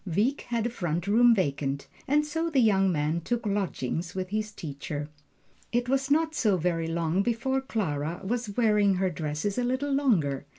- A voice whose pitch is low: No, high, 200 Hz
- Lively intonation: Yes, wide, 6.7 semitones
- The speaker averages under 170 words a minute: No, average, 175 wpm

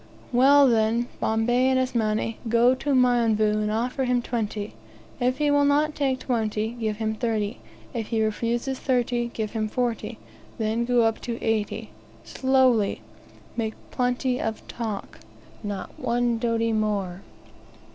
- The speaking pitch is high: Yes, high, 235 Hz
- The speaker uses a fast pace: No, average, 140 wpm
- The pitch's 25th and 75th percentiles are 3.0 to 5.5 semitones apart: No, narrow, 2.4 semitones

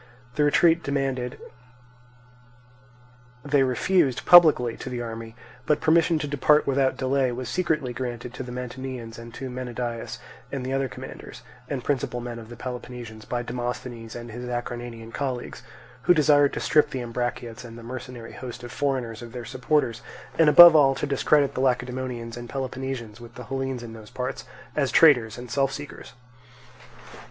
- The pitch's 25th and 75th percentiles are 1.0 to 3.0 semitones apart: Yes, narrow, 2.4 semitones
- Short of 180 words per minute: Yes, average, 165 wpm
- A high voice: No, low, 125 Hz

